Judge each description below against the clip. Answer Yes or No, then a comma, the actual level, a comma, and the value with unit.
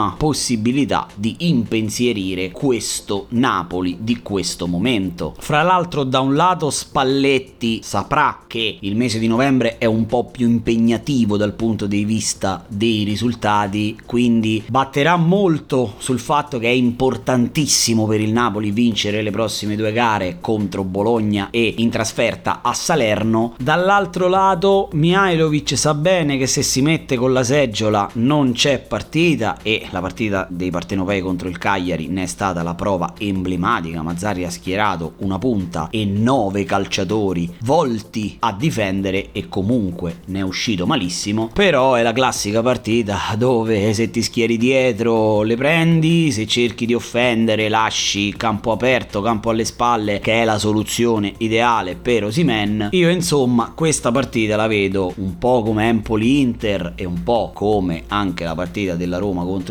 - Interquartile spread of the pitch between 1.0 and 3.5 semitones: No, average, 3.9 semitones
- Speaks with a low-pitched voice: Yes, low, 110 Hz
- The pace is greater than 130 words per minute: Yes, average, 150 wpm